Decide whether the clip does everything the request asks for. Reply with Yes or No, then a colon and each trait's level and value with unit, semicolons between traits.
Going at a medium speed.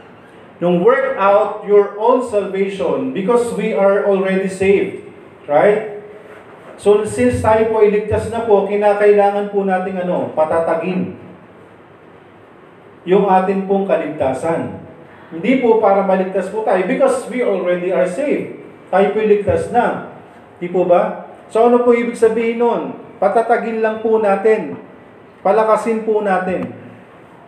Yes: average, 130 wpm